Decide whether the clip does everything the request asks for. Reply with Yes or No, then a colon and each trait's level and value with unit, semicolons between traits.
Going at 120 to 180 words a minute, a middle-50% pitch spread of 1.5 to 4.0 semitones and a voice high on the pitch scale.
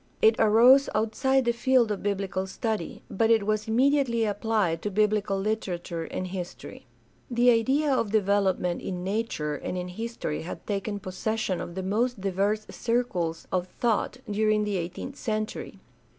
Yes: average, 150 wpm; average, 3.4 semitones; high, 210 Hz